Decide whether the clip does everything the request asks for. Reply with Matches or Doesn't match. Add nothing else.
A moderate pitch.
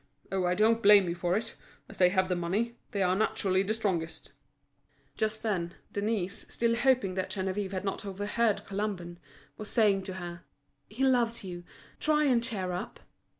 Doesn't match